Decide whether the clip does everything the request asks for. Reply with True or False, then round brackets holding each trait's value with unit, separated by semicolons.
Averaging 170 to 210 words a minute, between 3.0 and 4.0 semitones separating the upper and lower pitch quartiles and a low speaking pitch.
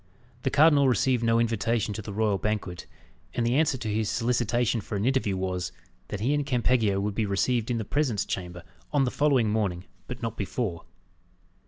True (190 wpm; 3.7 semitones; 115 Hz)